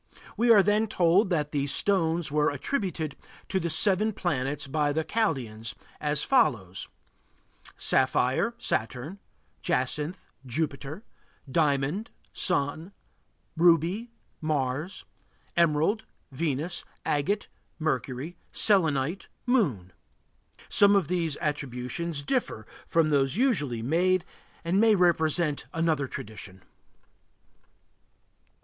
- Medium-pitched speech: Yes, medium, 160 Hz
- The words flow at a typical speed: No, slow, 95 wpm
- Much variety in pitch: No, average, 5.0 semitones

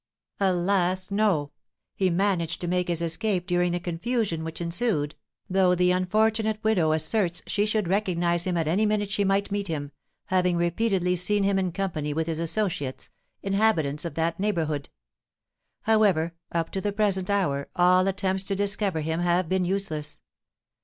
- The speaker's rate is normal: Yes, average, 160 wpm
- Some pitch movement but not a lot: Yes, average, 3.1 semitones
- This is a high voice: No, medium, 180 Hz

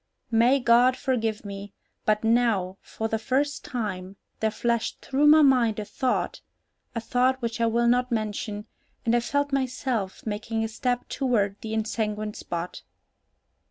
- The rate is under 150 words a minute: No, average, 155 wpm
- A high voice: Yes, high, 230 Hz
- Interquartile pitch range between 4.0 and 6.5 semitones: No, average, 2.9 semitones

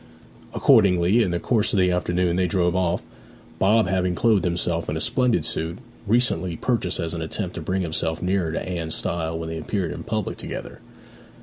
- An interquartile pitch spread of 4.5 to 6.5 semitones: No, average, 2.9 semitones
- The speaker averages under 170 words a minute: No, average, 190 wpm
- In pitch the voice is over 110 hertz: No, very low, 90 Hz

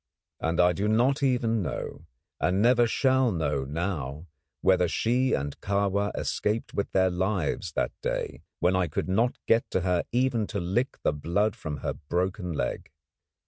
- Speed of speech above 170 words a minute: No, average, 165 wpm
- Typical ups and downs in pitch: Yes, average, 4.8 semitones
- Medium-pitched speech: No, very low, 95 Hz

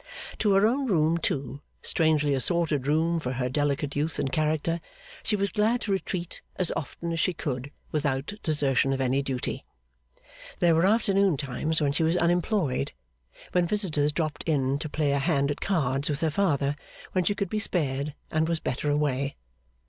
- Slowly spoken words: No, average, 180 wpm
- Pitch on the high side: No, medium, 155 Hz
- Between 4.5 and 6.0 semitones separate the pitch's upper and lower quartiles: No, average, 3.7 semitones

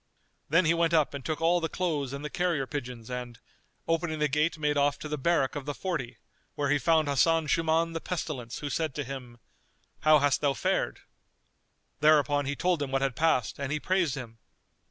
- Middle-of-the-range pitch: Yes, medium, 150 Hz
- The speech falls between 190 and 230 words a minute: Yes, fast, 205 wpm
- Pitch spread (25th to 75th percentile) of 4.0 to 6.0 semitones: No, average, 3.1 semitones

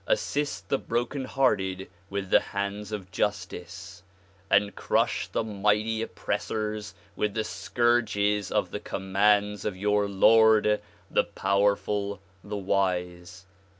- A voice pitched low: Yes, low, 105 Hz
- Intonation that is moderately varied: No, narrow, 1.7 semitones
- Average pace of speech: No, slow, 115 wpm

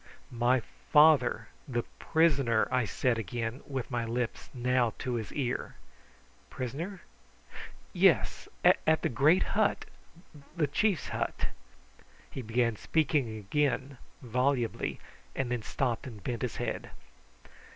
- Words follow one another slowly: Yes, slow, 120 wpm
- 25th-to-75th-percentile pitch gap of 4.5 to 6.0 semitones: No, average, 3.5 semitones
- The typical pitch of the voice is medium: No, low, 125 Hz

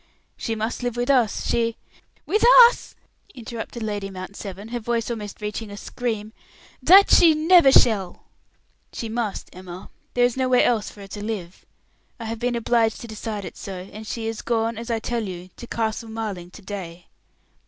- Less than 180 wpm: No, average, 185 wpm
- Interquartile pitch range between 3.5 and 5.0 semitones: No, average, 2.7 semitones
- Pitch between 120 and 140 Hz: No, high, 225 Hz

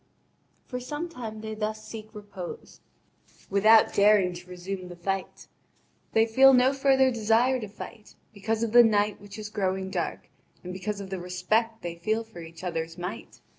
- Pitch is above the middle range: Yes, high, 210 Hz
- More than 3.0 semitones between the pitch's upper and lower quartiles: Yes, average, 3.4 semitones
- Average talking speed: Yes, average, 170 wpm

